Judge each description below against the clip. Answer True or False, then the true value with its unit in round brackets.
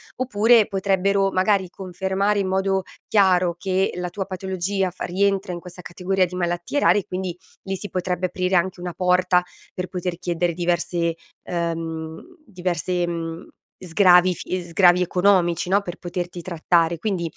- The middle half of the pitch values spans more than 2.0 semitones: False (1.7 semitones)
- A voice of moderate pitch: True (180 Hz)